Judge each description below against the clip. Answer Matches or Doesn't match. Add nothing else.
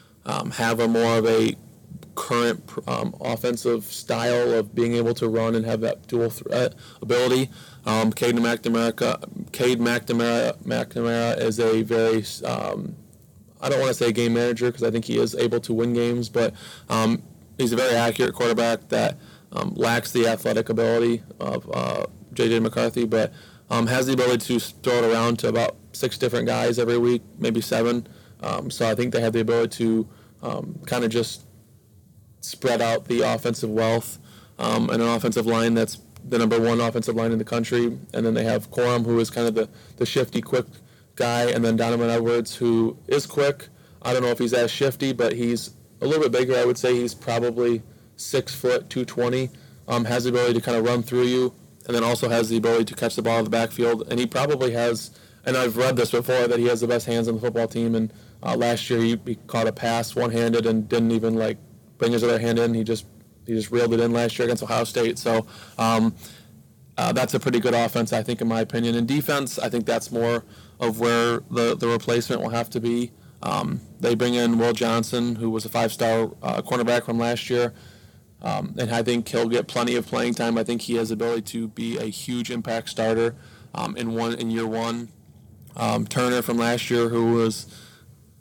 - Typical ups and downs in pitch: Doesn't match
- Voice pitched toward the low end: Matches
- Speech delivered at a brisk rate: Matches